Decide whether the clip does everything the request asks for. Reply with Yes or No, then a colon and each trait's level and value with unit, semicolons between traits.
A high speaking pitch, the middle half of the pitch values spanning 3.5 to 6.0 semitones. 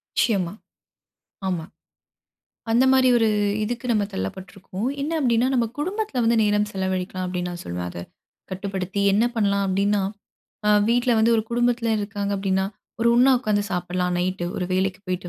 Yes: high, 200 Hz; average, 4.0 semitones